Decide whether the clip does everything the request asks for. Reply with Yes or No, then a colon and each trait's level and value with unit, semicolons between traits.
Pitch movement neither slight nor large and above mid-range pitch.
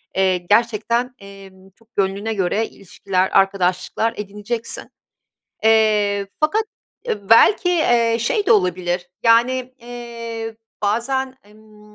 Yes: average, 3.1 semitones; high, 220 Hz